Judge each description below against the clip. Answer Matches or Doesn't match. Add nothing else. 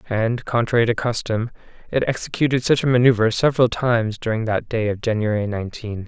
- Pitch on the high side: Doesn't match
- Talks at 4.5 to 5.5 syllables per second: Doesn't match